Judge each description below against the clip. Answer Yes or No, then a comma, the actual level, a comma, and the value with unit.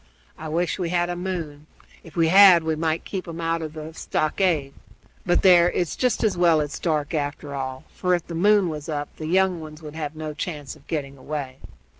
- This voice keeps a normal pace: No, fast, 215 wpm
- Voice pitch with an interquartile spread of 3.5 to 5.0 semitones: No, average, 2.7 semitones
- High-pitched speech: No, medium, 160 Hz